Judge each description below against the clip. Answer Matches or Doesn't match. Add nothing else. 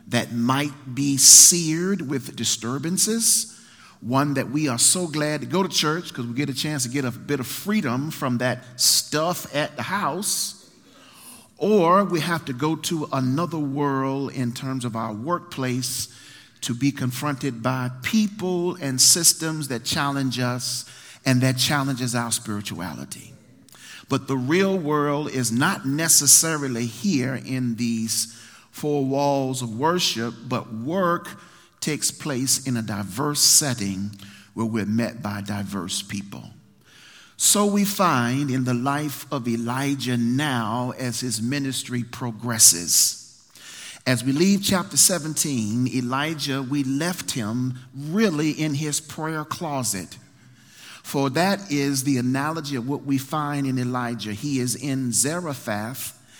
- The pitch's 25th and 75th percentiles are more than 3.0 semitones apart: Matches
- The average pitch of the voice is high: Doesn't match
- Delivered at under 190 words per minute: Matches